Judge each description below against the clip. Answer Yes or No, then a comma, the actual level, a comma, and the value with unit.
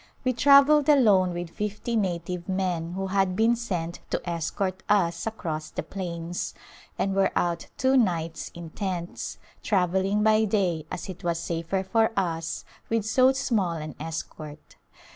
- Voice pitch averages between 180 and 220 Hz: Yes, medium, 185 Hz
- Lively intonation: No, average, 4.0 semitones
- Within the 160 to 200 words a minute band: No, average, 150 wpm